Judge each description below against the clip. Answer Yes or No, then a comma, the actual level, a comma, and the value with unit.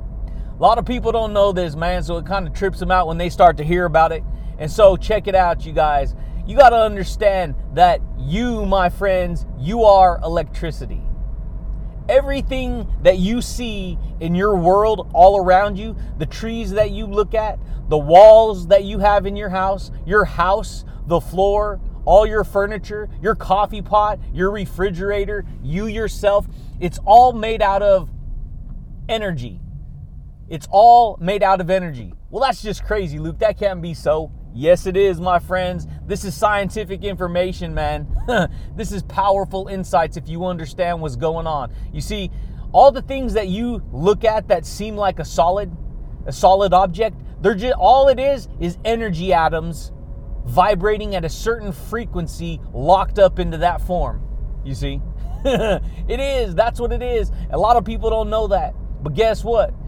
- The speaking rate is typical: Yes, average, 170 wpm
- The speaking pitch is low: No, high, 190 Hz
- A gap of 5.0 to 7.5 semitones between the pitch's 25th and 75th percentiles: No, average, 4.0 semitones